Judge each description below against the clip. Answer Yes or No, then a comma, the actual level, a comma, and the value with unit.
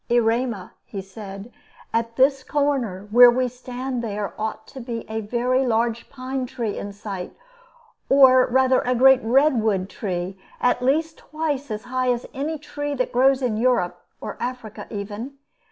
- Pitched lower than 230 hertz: No, high, 245 Hz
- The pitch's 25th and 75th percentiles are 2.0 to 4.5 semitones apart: Yes, average, 3.3 semitones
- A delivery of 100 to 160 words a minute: Yes, average, 155 wpm